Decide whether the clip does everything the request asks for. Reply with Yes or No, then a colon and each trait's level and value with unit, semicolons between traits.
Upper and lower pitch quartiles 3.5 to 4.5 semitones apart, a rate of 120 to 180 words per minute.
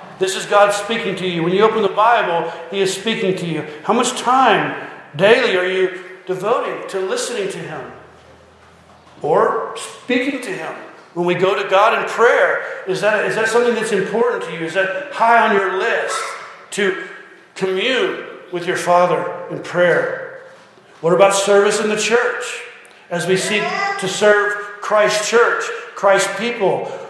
No: wide, 5.6 semitones; average, 165 wpm